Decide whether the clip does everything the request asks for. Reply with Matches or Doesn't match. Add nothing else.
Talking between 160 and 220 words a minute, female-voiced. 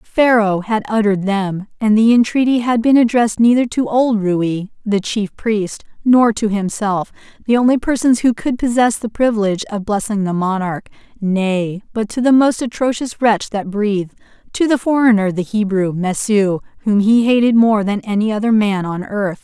Matches